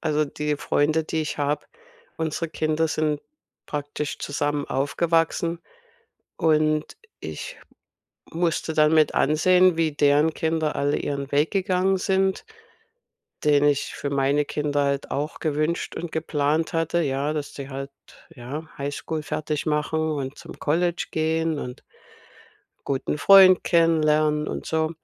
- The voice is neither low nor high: Yes, medium, 155 Hz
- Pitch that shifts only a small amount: Yes, narrow, 1.9 semitones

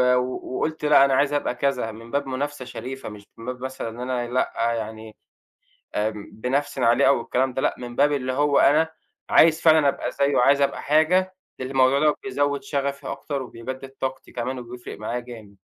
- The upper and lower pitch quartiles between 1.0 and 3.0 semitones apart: Yes, average, 2.7 semitones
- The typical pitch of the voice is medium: No, low, 130 Hz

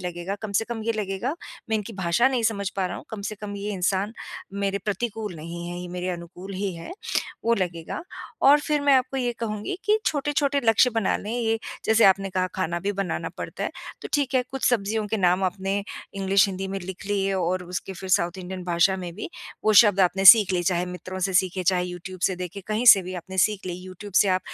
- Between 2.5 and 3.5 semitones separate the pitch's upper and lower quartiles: Yes, average, 3.1 semitones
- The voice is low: No, high, 195 Hz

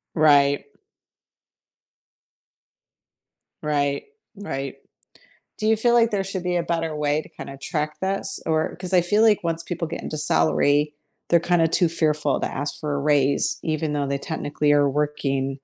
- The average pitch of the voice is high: No, medium, 155 Hz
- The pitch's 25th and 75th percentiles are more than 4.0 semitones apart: No, average, 3.4 semitones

